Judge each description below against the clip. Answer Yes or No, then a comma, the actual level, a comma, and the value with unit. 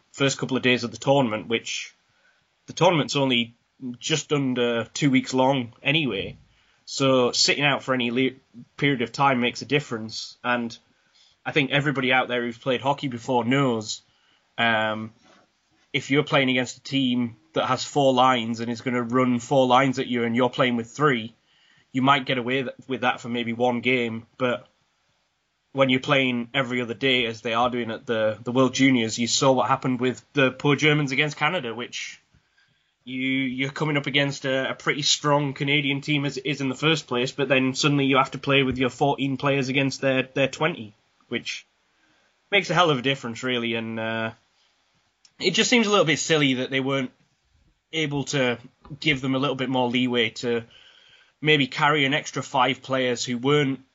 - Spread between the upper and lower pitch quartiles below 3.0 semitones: Yes, narrow, 2.4 semitones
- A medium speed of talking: Yes, average, 190 wpm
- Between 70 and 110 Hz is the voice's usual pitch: No, low, 130 Hz